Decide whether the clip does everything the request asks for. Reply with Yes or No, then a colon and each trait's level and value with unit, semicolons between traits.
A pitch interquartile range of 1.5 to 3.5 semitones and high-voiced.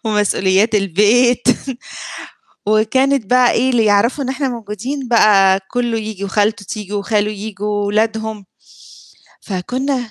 Yes: average, 3.1 semitones; high, 215 Hz